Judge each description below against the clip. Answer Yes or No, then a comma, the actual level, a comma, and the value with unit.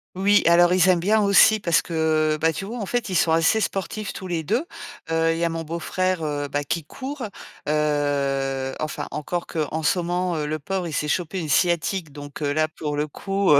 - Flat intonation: No, average, 3.6 semitones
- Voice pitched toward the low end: No, medium, 165 Hz